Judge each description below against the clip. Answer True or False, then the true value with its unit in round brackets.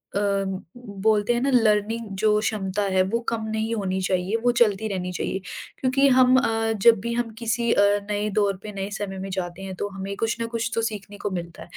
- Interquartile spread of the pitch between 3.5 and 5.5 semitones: False (2.9 semitones)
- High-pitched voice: True (215 Hz)